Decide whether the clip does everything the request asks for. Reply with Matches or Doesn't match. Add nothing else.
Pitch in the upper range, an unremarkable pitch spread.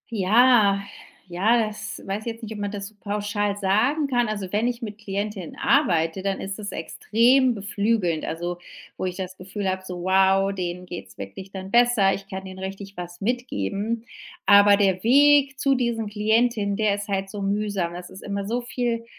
Matches